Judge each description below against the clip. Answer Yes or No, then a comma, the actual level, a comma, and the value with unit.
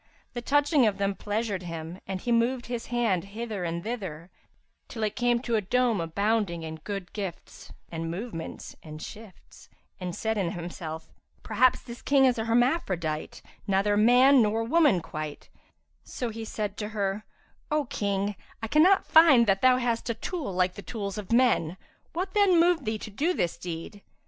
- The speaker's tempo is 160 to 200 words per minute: Yes, average, 175 wpm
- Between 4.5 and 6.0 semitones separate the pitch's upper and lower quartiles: Yes, average, 4.8 semitones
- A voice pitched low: No, high, 215 Hz